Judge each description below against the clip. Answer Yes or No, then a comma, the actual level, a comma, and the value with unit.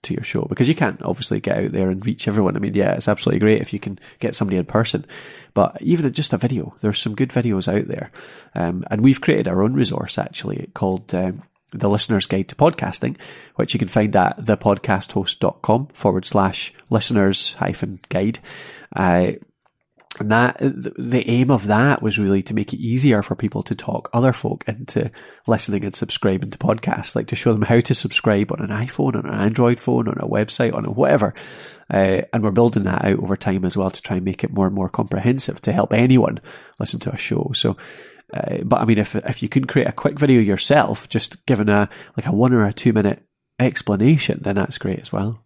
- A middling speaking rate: No, fast, 215 wpm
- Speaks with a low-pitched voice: Yes, low, 110 Hz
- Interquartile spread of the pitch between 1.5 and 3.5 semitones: No, average, 4.0 semitones